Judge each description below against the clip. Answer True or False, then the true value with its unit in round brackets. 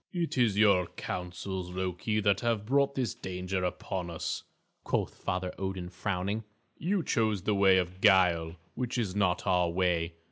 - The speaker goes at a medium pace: True (155 wpm)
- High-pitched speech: False (95 Hz)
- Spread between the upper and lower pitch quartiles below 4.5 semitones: True (2.9 semitones)